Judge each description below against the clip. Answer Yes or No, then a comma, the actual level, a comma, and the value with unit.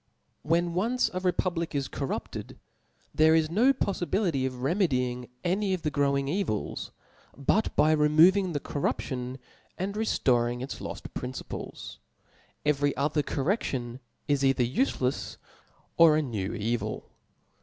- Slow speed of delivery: Yes, slow, 125 wpm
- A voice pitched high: No, medium, 150 Hz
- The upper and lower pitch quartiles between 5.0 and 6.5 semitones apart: Yes, wide, 5.6 semitones